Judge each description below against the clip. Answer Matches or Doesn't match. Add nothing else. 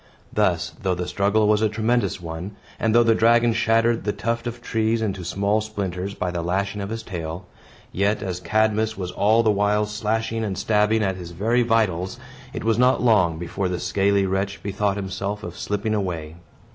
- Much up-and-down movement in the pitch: Doesn't match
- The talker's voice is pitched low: Matches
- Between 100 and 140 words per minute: Doesn't match